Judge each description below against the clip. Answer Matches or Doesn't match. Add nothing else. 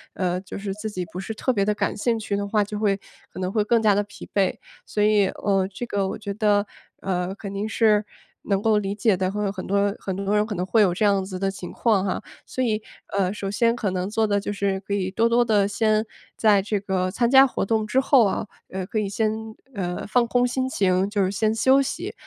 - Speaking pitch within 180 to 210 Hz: Matches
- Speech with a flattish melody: Matches